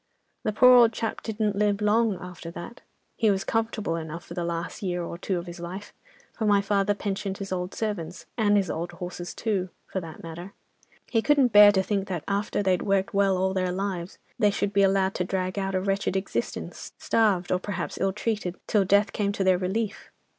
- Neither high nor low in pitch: No, high, 195 Hz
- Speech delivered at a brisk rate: Yes, fast, 210 wpm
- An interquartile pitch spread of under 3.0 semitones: Yes, narrow, 2.4 semitones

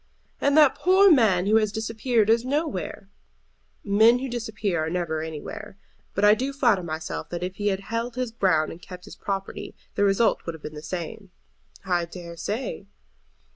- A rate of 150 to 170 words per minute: No, average, 180 wpm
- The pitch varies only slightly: No, average, 4.7 semitones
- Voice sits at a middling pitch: No, high, 205 Hz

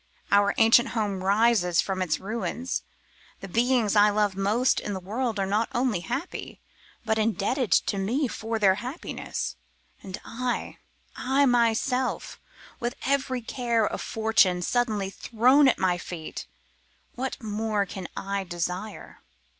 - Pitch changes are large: No, average, 3.8 semitones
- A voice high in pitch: Yes, high, 220 Hz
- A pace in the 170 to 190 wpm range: No, average, 140 wpm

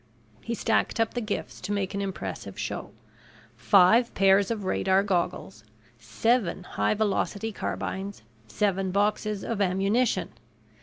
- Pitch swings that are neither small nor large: No, narrow, 2.3 semitones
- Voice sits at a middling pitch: No, high, 200 Hz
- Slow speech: Yes, slow, 125 wpm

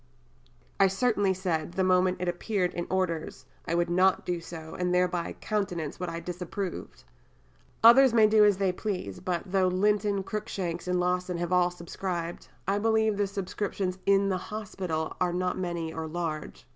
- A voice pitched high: No, medium, 180 Hz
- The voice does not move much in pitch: Yes, narrow, 2.3 semitones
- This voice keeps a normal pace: Yes, average, 170 wpm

